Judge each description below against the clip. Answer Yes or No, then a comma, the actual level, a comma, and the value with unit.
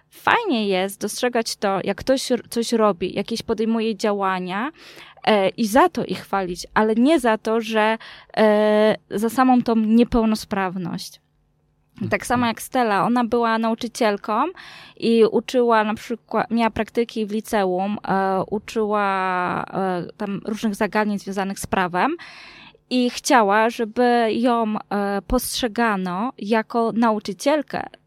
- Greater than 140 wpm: No, average, 125 wpm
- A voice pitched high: Yes, high, 220 Hz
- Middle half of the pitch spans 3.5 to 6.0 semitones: No, average, 2.8 semitones